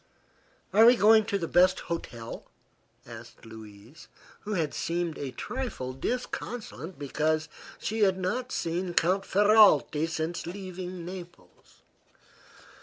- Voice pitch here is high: No, medium, 175 Hz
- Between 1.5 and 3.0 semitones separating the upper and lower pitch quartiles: No, average, 4.5 semitones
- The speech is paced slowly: Yes, slow, 115 wpm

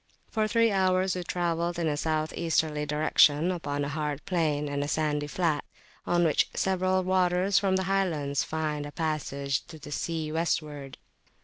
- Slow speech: No, average, 170 wpm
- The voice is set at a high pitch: No, medium, 160 Hz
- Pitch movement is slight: No, average, 3.7 semitones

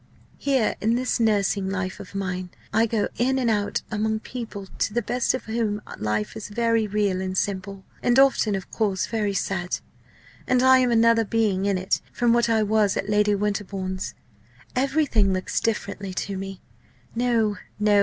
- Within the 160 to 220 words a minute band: Yes, average, 175 wpm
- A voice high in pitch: Yes, high, 210 Hz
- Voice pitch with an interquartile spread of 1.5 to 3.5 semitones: Yes, average, 2.9 semitones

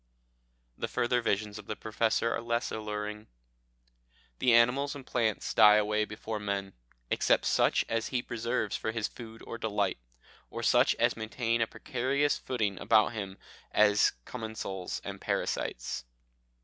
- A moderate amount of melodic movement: No, narrow, 2.0 semitones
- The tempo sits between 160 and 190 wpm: No, average, 145 wpm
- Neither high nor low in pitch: No, low, 110 Hz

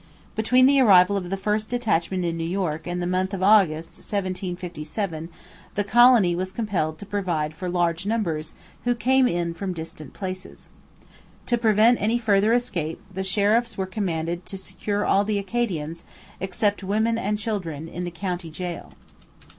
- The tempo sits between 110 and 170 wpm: Yes, average, 160 wpm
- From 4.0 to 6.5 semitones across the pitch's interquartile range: No, average, 3.6 semitones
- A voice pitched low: No, high, 190 Hz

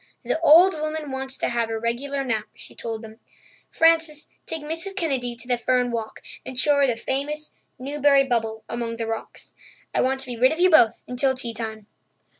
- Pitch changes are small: No, average, 4.3 semitones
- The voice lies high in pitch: Yes, very high, 260 Hz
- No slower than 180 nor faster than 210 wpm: Yes, average, 200 wpm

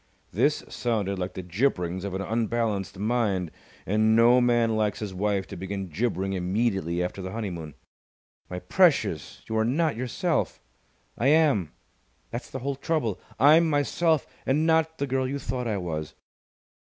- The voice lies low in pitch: Yes, low, 110 Hz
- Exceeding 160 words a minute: No, average, 155 wpm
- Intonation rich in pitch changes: Yes, wide, 5.8 semitones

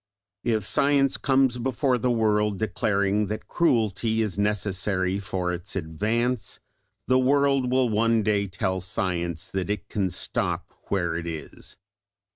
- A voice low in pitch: Yes, low, 105 Hz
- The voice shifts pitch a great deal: No, average, 4.2 semitones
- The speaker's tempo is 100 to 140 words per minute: Yes, slow, 135 wpm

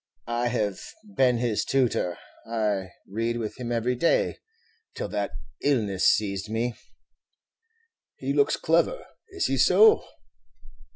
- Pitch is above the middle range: No, low, 115 Hz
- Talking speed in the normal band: No, slow, 120 wpm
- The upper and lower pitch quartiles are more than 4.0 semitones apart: No, average, 3.2 semitones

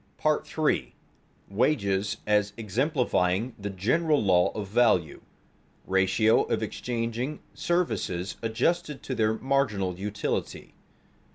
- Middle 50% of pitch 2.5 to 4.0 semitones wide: No, average, 4.9 semitones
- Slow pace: Yes, slow, 115 wpm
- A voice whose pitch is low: Yes, low, 110 Hz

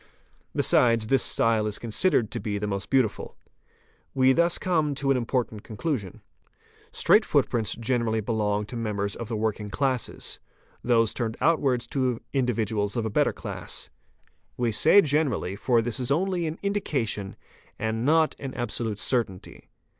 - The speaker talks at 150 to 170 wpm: Yes, average, 155 wpm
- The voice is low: Yes, low, 115 Hz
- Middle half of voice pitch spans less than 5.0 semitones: Yes, average, 3.9 semitones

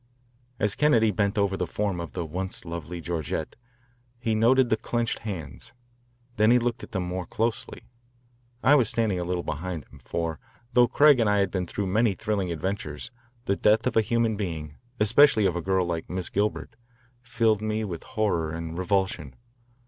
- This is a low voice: Yes, low, 100 Hz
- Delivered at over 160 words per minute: Yes, average, 180 wpm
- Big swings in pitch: No, average, 4.4 semitones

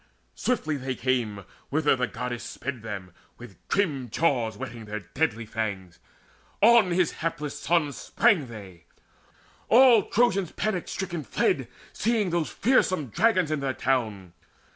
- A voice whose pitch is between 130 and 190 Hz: Yes, medium, 140 Hz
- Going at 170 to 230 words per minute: No, slow, 135 wpm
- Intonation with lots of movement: Yes, wide, 8.2 semitones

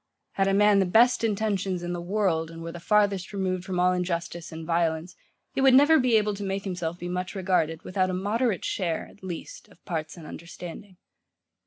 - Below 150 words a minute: No, fast, 205 wpm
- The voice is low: No, medium, 185 Hz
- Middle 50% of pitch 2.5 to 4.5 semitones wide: Yes, average, 3.0 semitones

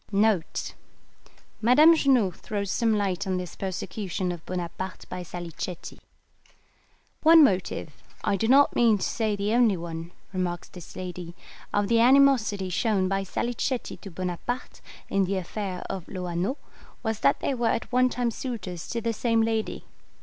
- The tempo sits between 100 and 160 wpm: Yes, average, 150 wpm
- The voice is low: No, high, 200 Hz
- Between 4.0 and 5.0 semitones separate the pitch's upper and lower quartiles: Yes, average, 4.4 semitones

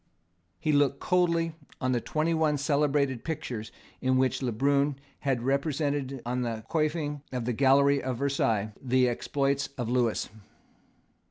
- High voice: No, medium, 140 Hz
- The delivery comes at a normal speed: Yes, average, 145 wpm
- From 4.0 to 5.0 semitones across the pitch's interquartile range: No, average, 2.7 semitones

